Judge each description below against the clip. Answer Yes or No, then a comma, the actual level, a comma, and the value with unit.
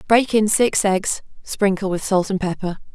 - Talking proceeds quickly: No, average, 185 wpm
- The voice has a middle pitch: No, high, 195 Hz